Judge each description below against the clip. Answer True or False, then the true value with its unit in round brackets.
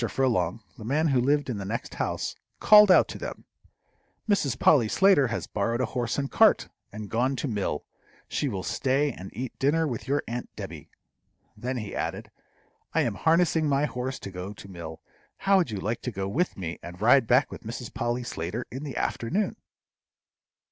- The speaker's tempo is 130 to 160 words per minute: False (190 wpm)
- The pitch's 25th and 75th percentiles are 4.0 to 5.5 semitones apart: True (5.0 semitones)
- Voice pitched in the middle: False (125 Hz)